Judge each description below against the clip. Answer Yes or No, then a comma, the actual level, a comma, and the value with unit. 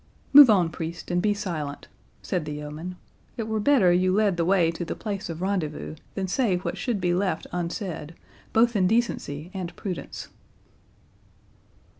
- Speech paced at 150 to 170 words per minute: Yes, average, 165 wpm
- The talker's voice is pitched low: No, medium, 185 Hz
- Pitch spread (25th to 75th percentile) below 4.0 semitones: Yes, average, 3.5 semitones